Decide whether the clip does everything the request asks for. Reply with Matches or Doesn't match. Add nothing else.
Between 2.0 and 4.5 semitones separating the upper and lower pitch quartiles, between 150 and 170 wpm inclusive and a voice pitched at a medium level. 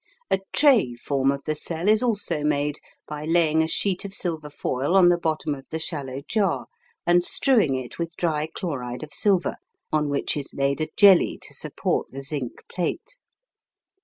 Doesn't match